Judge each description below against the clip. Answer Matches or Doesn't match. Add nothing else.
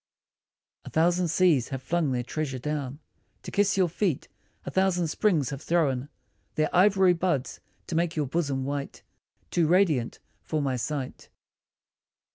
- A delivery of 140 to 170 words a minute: Matches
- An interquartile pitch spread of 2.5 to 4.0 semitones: Doesn't match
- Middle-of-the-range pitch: Matches